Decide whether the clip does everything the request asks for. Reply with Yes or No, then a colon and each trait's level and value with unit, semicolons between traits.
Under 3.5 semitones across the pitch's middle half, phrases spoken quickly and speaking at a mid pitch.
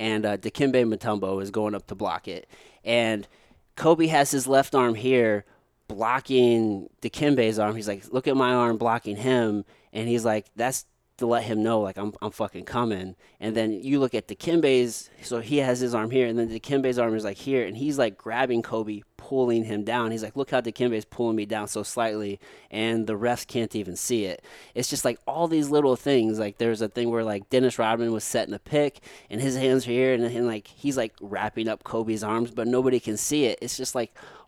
No: average, 2.9 semitones; fast, 220 wpm; low, 115 Hz